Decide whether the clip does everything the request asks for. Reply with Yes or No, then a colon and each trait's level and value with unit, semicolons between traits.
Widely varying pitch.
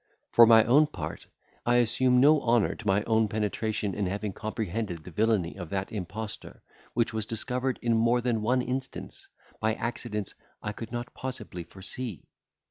No: narrow, 2.6 semitones